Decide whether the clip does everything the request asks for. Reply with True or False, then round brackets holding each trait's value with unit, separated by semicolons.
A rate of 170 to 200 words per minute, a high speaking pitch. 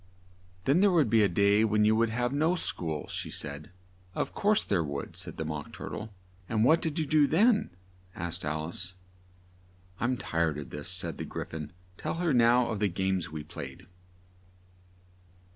False (180 wpm; 105 Hz)